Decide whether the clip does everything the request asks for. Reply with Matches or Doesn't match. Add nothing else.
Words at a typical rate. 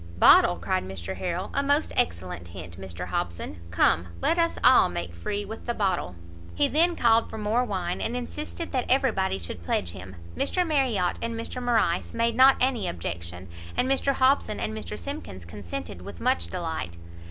Matches